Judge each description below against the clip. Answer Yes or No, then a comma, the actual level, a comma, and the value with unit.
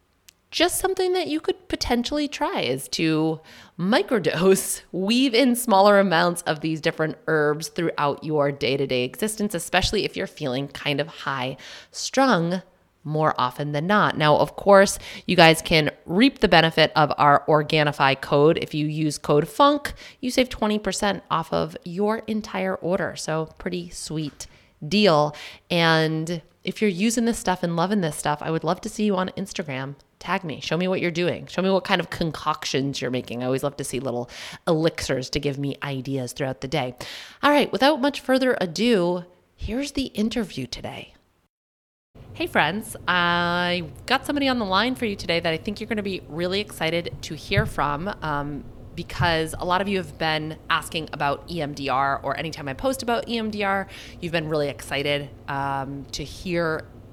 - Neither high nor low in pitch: Yes, medium, 170 Hz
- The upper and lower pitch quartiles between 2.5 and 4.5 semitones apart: No, wide, 5.6 semitones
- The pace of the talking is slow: No, average, 180 wpm